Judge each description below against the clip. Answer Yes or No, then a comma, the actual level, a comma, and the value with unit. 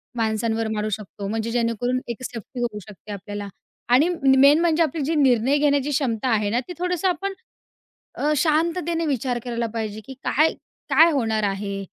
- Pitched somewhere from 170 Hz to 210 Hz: No, high, 245 Hz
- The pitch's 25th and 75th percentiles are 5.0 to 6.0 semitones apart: Yes, wide, 5.4 semitones